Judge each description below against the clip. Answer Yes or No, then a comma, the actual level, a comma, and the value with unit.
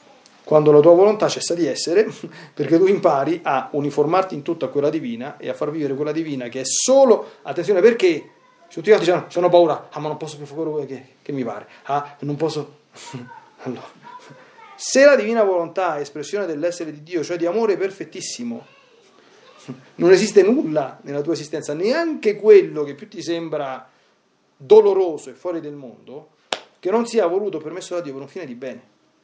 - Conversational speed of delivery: No, fast, 180 wpm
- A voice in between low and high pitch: Yes, medium, 170 Hz